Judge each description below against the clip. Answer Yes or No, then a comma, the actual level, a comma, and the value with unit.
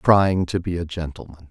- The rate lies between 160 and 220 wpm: Yes, average, 200 wpm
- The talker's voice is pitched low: Yes, very low, 85 Hz